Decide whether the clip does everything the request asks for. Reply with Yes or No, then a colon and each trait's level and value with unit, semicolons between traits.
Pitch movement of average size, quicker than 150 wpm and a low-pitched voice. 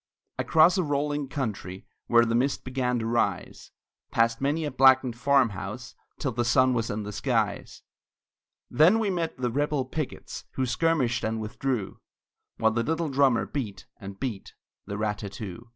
Yes: average, 4.1 semitones; average, 165 wpm; low, 125 Hz